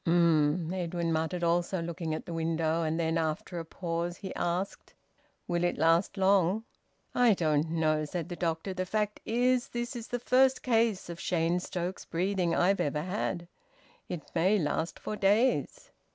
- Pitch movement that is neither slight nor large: Yes, average, 3.1 semitones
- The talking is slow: No, average, 165 wpm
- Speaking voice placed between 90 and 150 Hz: No, medium, 175 Hz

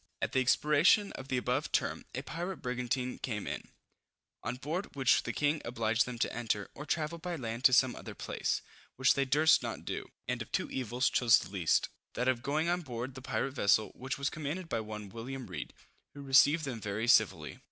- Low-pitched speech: Yes, low, 130 Hz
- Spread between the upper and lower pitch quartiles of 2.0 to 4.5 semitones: Yes, average, 3.7 semitones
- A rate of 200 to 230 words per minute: Yes, fast, 205 wpm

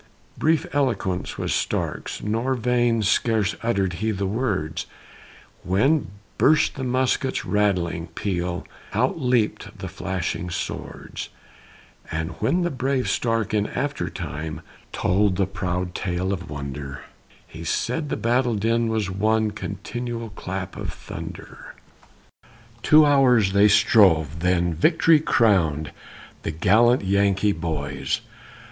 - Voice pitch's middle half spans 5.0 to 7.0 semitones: Yes, average, 5.3 semitones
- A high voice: No, low, 100 Hz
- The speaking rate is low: Yes, slow, 120 wpm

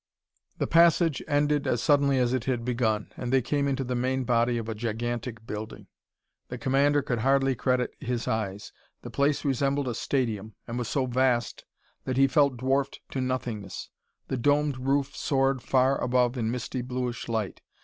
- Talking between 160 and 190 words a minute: Yes, average, 175 wpm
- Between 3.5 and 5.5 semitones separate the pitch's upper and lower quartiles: No, narrow, 2.5 semitones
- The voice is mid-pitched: No, low, 130 Hz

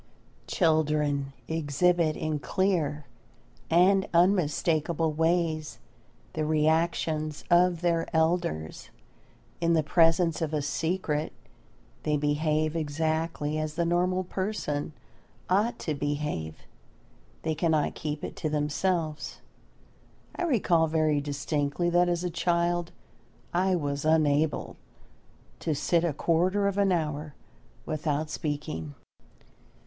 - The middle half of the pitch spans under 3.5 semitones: Yes, narrow, 2.5 semitones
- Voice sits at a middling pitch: Yes, medium, 160 Hz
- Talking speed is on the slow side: Yes, slow, 110 wpm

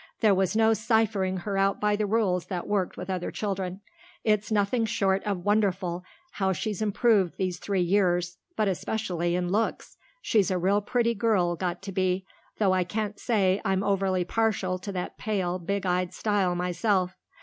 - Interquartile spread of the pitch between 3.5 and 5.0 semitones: No, narrow, 2.5 semitones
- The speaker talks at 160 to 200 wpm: Yes, average, 175 wpm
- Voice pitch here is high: Yes, high, 195 Hz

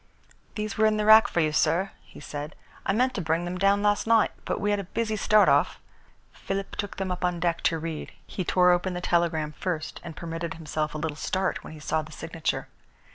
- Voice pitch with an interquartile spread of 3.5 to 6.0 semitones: Yes, average, 3.9 semitones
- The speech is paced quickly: Yes, fast, 230 wpm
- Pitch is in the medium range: Yes, medium, 180 Hz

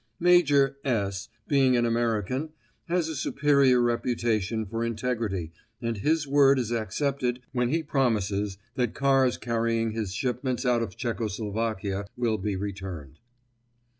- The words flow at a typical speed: No, slow, 130 wpm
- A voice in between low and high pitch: No, low, 120 Hz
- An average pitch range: Yes, average, 3.9 semitones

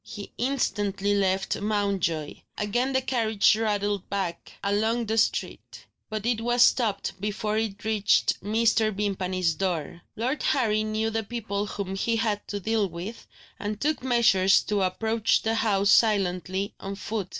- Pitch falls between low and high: No, high, 210 Hz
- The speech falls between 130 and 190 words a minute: Yes, average, 150 wpm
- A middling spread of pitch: No, narrow, 2.3 semitones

